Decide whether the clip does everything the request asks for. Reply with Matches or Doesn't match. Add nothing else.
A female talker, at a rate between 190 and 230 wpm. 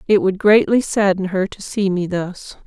Matches